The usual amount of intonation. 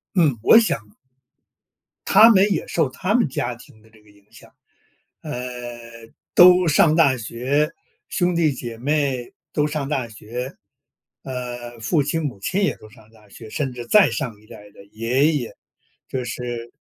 Yes: average, 5.0 semitones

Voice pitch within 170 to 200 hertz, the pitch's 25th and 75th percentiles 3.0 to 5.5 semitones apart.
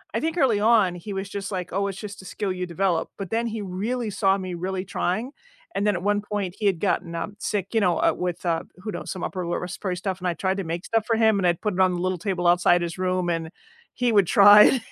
No: high, 190 Hz; narrow, 2.6 semitones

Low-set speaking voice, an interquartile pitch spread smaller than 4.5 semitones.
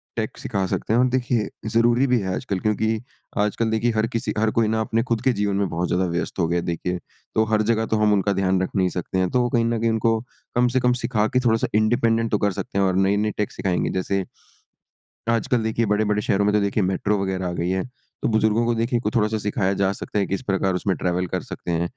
Yes: low, 105 Hz; average, 3.1 semitones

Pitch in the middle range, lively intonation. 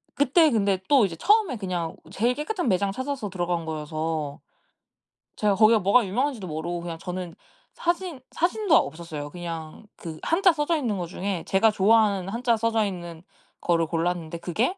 No: high, 195 Hz; wide, 6.6 semitones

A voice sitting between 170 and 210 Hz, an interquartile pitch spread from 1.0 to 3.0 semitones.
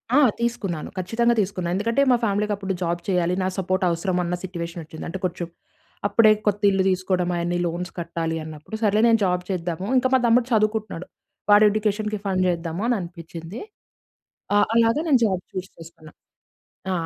No: medium, 185 Hz; average, 3.7 semitones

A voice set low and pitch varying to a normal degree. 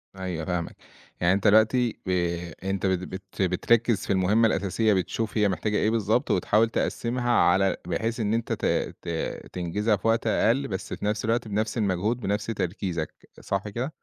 Yes: low, 105 Hz; average, 3.2 semitones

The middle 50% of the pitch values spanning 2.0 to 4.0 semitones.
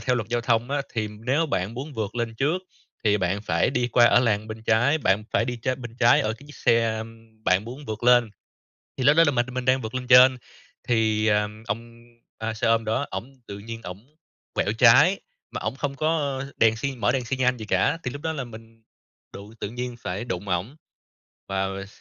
Yes: average, 3.1 semitones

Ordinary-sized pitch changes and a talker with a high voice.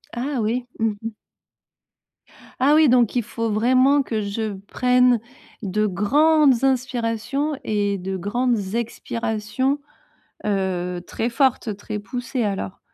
Yes: average, 3.6 semitones; high, 230 Hz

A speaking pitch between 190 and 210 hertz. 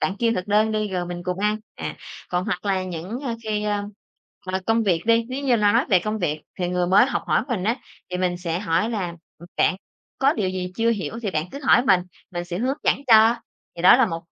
Yes: high, 200 Hz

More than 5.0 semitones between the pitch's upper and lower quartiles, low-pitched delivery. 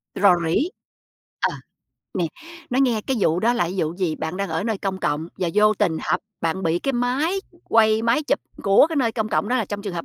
No: wide, 5.4 semitones; high, 205 Hz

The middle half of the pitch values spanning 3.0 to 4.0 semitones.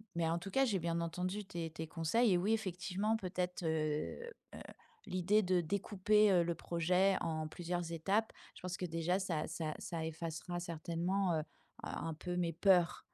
No: narrow, 2.4 semitones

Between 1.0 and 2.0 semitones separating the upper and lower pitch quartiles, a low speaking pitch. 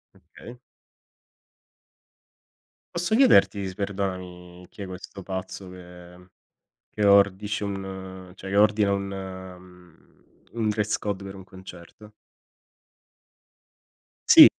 Yes: narrow, 1.7 semitones; very low, 95 Hz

